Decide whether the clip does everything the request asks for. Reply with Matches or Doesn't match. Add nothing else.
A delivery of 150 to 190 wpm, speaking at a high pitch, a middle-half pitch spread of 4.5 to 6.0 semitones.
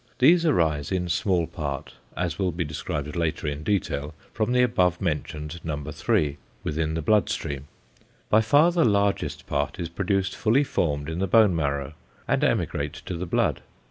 Doesn't match